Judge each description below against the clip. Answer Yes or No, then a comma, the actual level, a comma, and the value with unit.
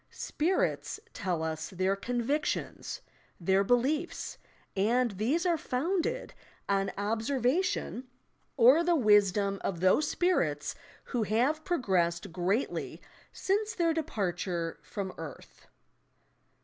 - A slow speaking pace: Yes, slow, 100 wpm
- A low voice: No, high, 225 Hz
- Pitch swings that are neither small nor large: No, wide, 8.3 semitones